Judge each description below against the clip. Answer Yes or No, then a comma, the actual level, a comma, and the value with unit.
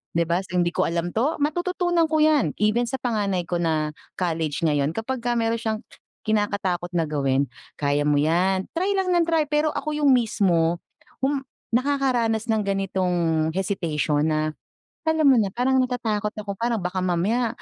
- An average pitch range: No, wide, 7.0 semitones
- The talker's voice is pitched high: Yes, high, 205 Hz